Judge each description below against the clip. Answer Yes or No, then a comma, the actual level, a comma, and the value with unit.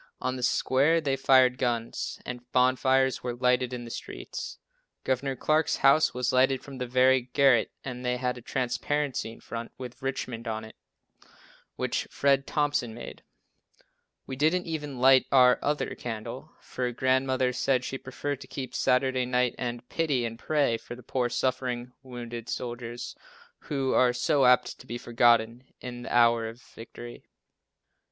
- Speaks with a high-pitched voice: No, low, 125 Hz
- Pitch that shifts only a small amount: Yes, narrow, 1.7 semitones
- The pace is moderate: Yes, average, 160 wpm